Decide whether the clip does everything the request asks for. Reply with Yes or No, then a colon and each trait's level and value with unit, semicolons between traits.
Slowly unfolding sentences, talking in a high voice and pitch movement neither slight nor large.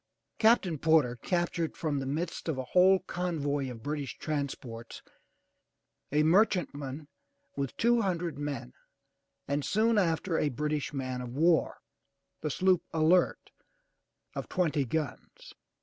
No: slow, 125 wpm; medium, 155 Hz; average, 4.0 semitones